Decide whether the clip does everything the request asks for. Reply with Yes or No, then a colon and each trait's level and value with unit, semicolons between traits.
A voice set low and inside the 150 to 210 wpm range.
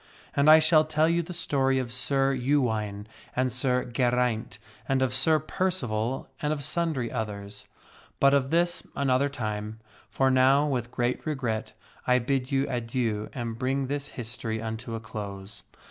Yes: low, 130 Hz; average, 160 wpm